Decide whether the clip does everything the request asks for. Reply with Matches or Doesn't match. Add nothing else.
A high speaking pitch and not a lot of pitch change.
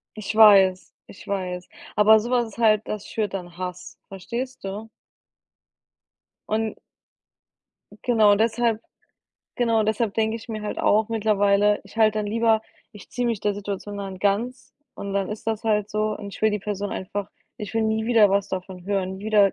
Matches